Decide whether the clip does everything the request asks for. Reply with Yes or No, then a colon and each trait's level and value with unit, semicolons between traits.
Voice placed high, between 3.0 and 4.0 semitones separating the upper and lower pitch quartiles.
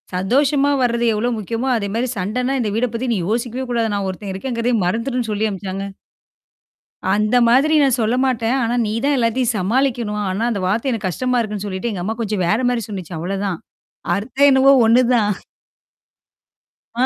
Yes: high, 230 Hz; average, 3.6 semitones